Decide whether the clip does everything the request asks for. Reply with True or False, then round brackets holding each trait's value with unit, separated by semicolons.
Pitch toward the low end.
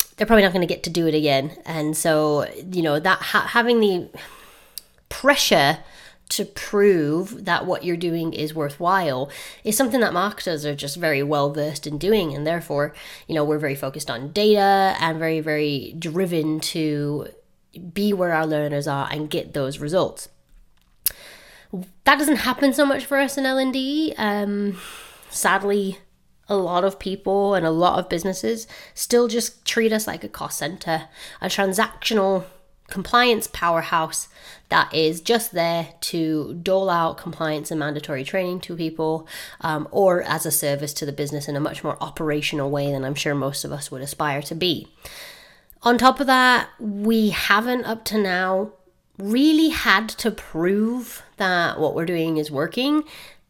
False (175 Hz)